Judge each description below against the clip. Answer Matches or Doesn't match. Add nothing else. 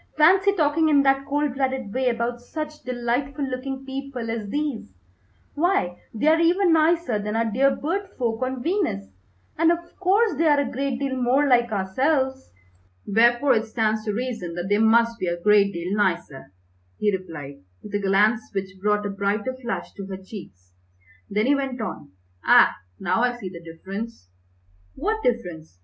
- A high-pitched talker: Matches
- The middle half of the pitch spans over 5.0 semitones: Matches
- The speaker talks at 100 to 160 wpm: Doesn't match